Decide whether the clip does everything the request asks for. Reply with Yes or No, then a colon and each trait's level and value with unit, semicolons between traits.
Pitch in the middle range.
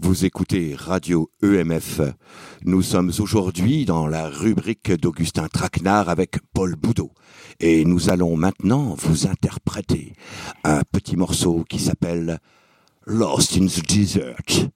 No: very low, 90 Hz